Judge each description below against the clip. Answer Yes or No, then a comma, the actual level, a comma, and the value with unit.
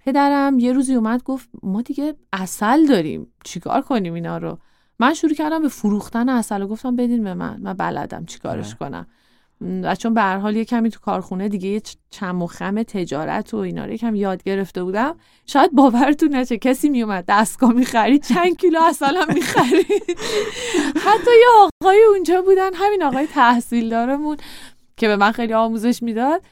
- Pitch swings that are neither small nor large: No, wide, 6.2 semitones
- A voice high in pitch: Yes, high, 245 Hz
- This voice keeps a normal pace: No, fast, 180 wpm